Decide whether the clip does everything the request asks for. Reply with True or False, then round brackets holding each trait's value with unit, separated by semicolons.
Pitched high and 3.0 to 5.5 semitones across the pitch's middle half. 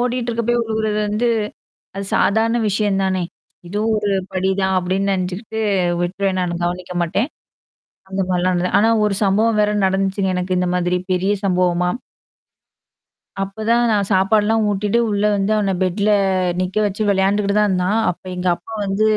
False (195 Hz; 2.5 semitones)